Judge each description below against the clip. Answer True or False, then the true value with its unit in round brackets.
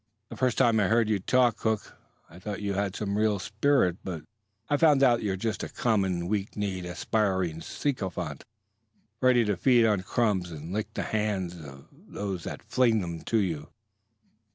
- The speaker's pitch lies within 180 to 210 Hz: False (105 Hz)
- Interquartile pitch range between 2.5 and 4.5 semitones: True (3.7 semitones)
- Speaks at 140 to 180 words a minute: True (175 wpm)